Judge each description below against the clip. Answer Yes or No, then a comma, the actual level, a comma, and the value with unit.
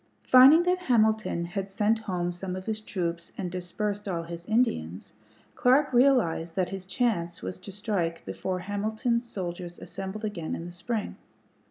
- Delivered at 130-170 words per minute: Yes, average, 160 wpm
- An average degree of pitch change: Yes, average, 4.0 semitones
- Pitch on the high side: Yes, high, 195 Hz